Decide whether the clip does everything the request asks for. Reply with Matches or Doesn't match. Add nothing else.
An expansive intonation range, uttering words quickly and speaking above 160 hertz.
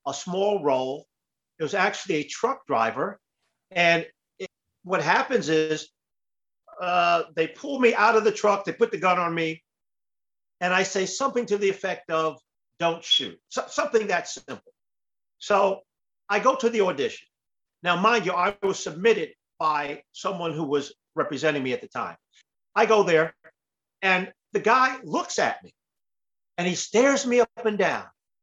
Doesn't match